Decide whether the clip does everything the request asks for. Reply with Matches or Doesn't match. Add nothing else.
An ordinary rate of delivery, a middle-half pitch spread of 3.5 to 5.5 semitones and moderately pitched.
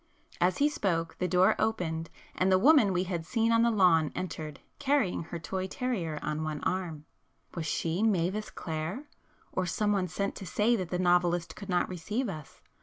Matches